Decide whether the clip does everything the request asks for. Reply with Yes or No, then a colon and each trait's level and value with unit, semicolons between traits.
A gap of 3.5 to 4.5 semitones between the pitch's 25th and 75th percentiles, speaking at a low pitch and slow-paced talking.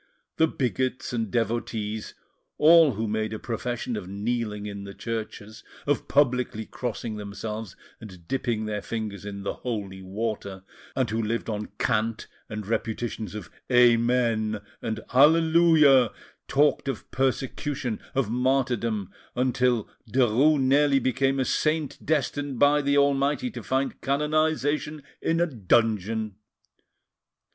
Yes: average, 4.1 semitones; low, 120 Hz; slow, 125 wpm